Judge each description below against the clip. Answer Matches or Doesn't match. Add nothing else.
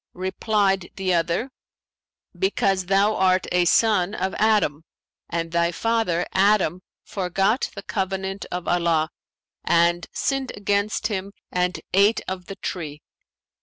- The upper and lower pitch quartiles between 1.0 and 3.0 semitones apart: Matches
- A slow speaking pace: Matches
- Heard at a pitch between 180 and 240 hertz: Matches